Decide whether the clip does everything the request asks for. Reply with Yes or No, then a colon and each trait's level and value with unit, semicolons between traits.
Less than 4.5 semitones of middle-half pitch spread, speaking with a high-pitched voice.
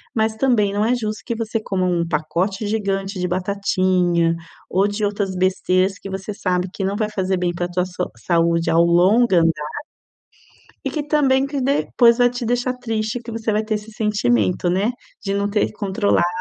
Yes: average, 3.5 semitones; high, 200 Hz